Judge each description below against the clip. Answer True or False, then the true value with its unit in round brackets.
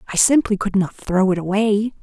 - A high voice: True (205 Hz)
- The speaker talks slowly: False (205 wpm)